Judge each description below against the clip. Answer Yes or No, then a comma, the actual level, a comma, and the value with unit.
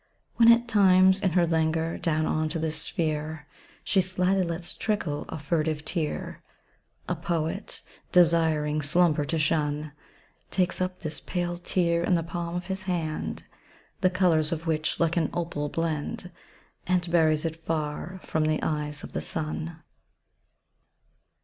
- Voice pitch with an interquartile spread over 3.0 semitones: No, narrow, 2.5 semitones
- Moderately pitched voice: Yes, medium, 165 Hz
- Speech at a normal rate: Yes, average, 150 wpm